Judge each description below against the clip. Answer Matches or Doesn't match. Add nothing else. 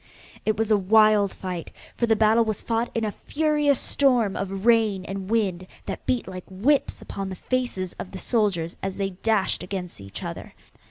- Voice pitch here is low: Doesn't match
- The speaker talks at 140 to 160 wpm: Doesn't match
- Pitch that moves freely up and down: Doesn't match